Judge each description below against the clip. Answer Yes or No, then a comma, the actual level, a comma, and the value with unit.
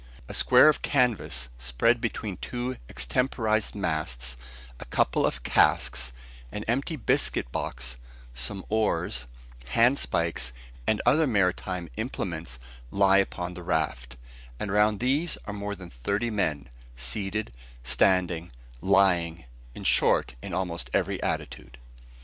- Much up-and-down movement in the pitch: Yes, wide, 8.3 semitones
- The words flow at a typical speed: No, slow, 120 wpm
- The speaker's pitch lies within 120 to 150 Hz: No, very low, 95 Hz